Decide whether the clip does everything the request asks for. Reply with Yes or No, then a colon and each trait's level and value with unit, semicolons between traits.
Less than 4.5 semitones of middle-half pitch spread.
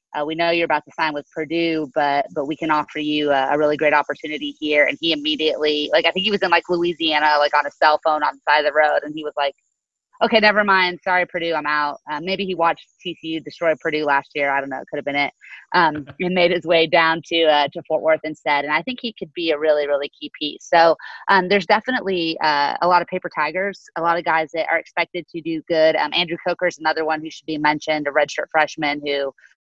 Yes: narrow, 2.5 semitones